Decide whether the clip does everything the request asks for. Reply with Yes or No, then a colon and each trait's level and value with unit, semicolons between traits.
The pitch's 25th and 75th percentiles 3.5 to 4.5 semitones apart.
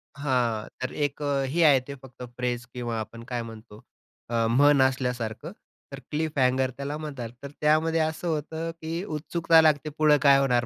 Yes: average, 3.8 semitones